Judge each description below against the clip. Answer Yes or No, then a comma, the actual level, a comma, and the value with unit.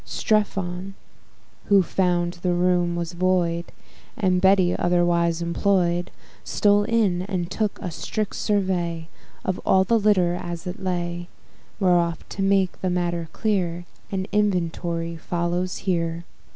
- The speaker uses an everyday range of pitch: No, narrow, 2.0 semitones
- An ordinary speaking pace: No, slow, 125 wpm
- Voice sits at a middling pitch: Yes, medium, 180 Hz